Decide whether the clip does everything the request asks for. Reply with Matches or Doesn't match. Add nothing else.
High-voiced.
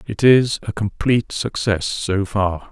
Doesn't match